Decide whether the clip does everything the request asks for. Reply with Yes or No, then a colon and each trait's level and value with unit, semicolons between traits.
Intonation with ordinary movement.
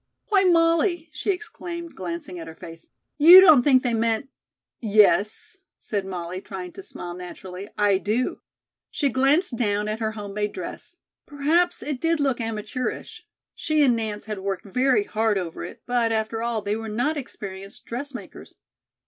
No: wide, 6.2 semitones